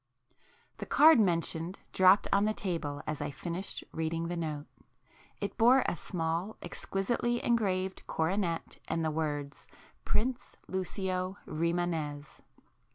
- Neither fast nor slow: No, slow, 120 wpm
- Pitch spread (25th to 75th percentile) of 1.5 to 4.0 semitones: Yes, average, 3.4 semitones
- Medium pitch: Yes, medium, 175 Hz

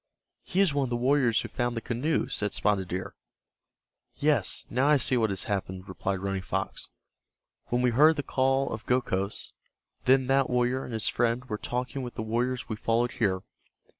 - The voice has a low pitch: Yes, low, 120 Hz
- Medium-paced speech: Yes, average, 190 wpm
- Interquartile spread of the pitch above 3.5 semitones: Yes, average, 3.9 semitones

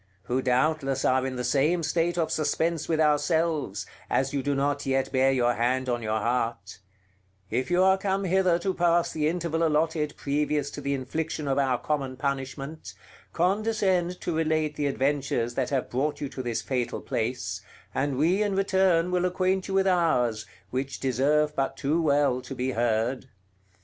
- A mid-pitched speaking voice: Yes, medium, 145 Hz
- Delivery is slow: No, average, 175 wpm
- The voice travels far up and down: No, average, 4.3 semitones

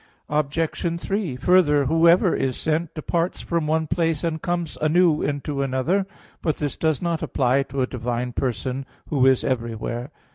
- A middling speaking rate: Yes, average, 155 wpm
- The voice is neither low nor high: Yes, medium, 150 Hz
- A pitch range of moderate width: Yes, average, 4.2 semitones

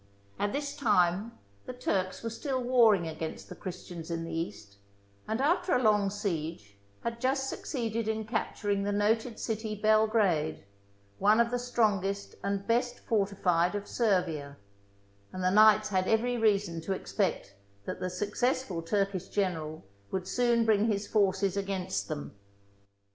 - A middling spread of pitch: Yes, average, 3.9 semitones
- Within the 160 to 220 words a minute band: No, average, 150 wpm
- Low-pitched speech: No, high, 205 Hz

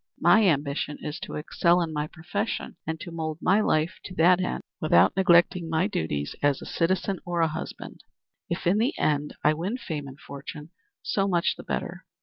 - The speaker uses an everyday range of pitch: Yes, average, 3.4 semitones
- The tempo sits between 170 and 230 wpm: Yes, average, 190 wpm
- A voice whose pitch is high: No, medium, 165 Hz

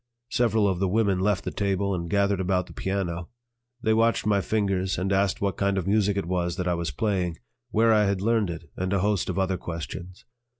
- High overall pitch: No, very low, 95 Hz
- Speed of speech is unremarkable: No, fast, 220 wpm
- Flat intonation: Yes, narrow, 2.1 semitones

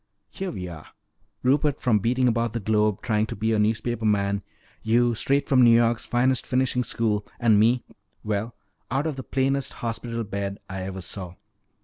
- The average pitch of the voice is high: No, low, 115 Hz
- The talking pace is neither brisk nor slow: Yes, average, 170 wpm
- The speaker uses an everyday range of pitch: Yes, average, 3.2 semitones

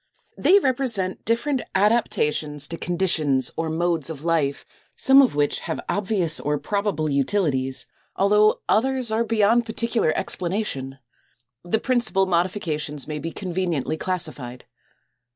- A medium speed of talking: No, slow, 120 wpm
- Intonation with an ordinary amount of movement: No, wide, 6.2 semitones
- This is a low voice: No, medium, 180 Hz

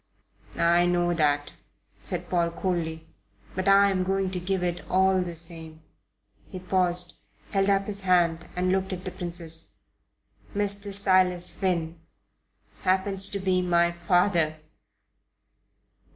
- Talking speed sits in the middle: No, slow, 130 wpm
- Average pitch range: No, narrow, 1.9 semitones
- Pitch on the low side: No, medium, 180 Hz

